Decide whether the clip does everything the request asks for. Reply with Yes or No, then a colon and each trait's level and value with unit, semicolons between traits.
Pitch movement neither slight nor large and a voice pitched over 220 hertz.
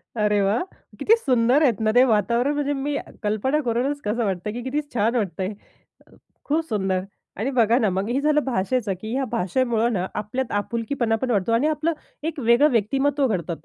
Yes: average, 4.5 semitones; high, 235 Hz